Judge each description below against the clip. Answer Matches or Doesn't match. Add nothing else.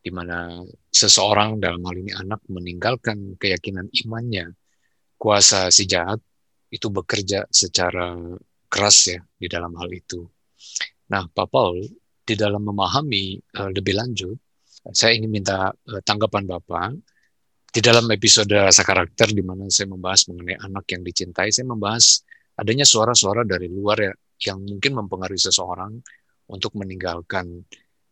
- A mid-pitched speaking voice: Doesn't match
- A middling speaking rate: Matches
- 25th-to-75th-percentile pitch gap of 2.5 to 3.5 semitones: Matches